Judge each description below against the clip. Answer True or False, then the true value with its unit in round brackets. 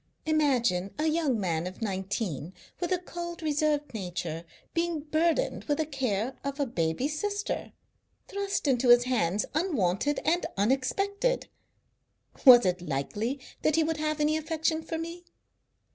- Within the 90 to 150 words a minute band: True (145 wpm)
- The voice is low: False (285 Hz)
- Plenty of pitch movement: True (7.9 semitones)